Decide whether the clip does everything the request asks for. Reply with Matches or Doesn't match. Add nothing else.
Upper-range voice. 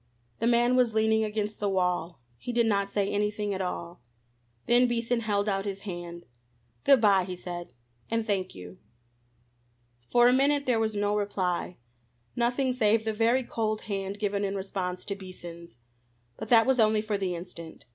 Matches